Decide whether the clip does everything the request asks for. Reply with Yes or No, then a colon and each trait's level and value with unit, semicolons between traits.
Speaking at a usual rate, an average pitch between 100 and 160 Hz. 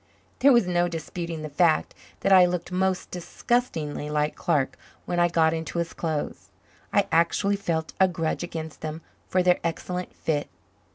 No: average, 165 wpm; medium, 170 Hz